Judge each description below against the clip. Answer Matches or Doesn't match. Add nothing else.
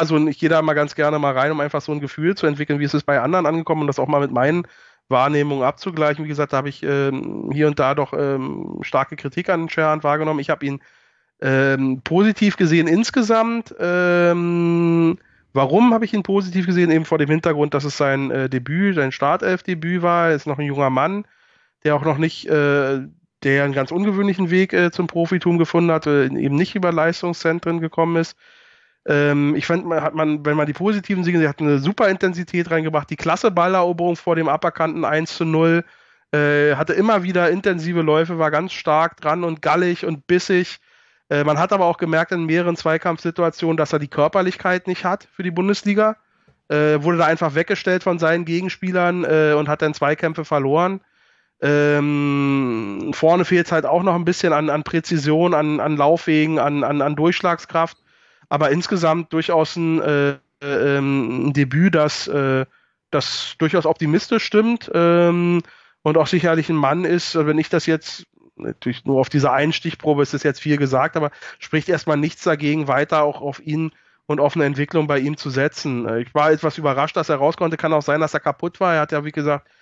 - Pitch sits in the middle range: Matches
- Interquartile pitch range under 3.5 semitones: Matches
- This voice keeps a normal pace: Doesn't match